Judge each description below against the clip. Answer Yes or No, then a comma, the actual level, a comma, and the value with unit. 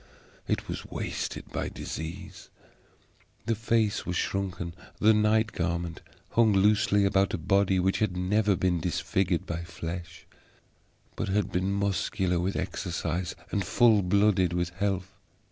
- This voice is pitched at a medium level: No, very low, 95 Hz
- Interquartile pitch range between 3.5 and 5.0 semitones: No, narrow, 2.6 semitones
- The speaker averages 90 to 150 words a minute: Yes, slow, 135 wpm